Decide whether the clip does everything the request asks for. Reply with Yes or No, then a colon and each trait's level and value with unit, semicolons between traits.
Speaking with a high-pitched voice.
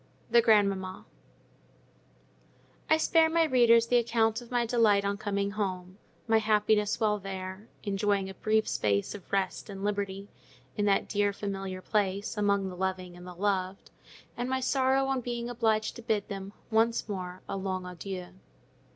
Yes: high, 205 Hz